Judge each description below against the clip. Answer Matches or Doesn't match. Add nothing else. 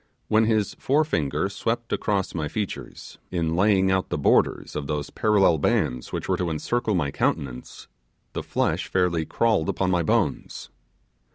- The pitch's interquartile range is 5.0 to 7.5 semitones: Matches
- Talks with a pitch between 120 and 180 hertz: Doesn't match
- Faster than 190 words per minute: Doesn't match